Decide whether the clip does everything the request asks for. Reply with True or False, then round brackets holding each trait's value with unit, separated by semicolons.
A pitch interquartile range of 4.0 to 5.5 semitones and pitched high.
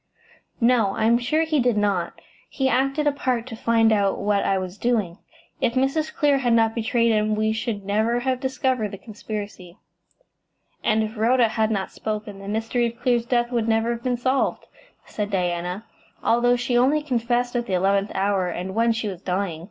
False (3.3 semitones; 225 Hz)